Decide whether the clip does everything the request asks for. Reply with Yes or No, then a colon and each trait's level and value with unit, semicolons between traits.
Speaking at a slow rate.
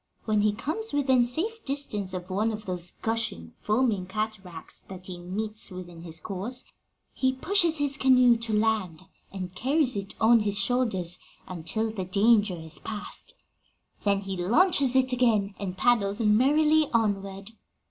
No: average, 155 wpm